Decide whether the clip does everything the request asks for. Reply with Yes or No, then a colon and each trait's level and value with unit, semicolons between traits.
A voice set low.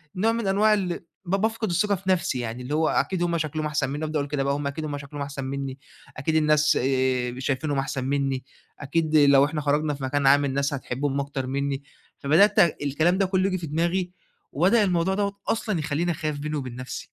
No: medium, 150 Hz